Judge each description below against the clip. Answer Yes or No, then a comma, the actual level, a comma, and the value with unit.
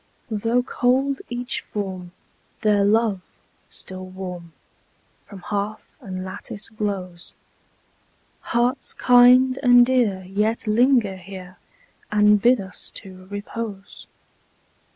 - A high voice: Yes, high, 210 Hz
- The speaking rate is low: Yes, slow, 100 wpm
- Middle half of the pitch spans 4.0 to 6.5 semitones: Yes, average, 4.3 semitones